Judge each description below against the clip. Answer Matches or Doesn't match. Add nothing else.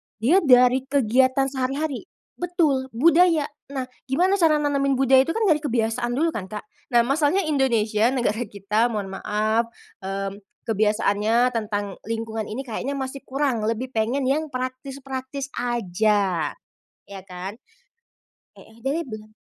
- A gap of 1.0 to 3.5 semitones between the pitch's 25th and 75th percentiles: Doesn't match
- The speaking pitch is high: Matches